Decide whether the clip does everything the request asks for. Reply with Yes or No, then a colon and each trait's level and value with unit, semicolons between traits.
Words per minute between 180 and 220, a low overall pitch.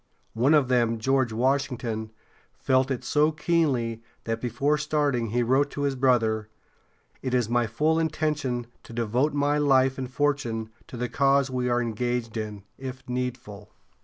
No: average, 160 wpm; low, 125 Hz